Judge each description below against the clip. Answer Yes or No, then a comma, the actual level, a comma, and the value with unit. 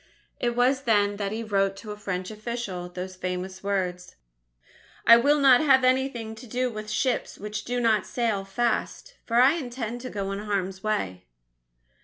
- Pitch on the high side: Yes, high, 215 Hz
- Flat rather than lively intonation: No, average, 3.8 semitones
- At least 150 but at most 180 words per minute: Yes, average, 175 wpm